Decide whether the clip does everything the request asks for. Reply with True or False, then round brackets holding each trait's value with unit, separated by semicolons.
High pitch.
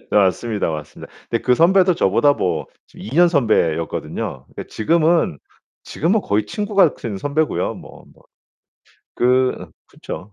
False (125 Hz)